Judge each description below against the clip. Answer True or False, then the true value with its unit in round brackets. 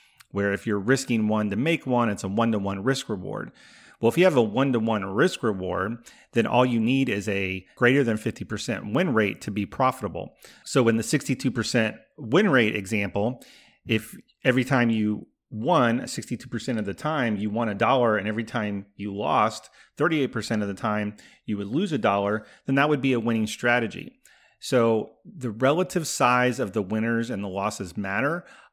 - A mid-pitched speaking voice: False (115 Hz)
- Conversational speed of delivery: True (190 wpm)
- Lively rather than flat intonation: False (3.3 semitones)